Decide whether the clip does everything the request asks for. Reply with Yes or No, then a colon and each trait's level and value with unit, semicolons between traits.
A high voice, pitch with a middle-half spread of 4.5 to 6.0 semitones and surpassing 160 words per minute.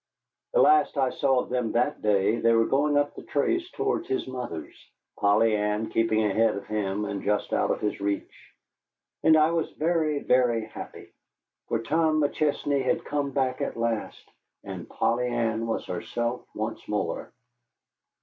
No: low, 120 Hz; average, 5.1 semitones; average, 170 wpm